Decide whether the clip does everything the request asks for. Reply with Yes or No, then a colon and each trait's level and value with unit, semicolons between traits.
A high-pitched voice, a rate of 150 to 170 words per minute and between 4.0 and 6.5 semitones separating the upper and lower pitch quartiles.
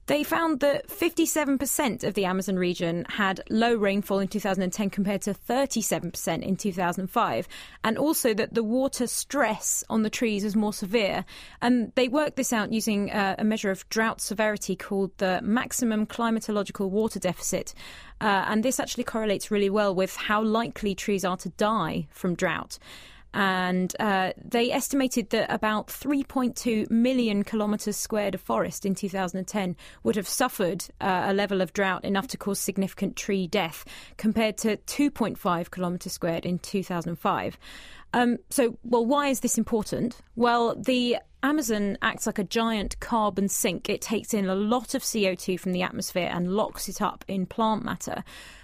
No: high, 210 Hz; average, 160 wpm; average, 3.5 semitones